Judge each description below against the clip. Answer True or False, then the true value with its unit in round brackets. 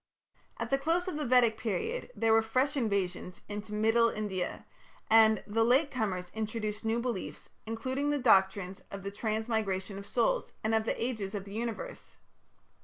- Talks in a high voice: True (220 Hz)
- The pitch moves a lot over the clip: False (3.4 semitones)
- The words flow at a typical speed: True (170 wpm)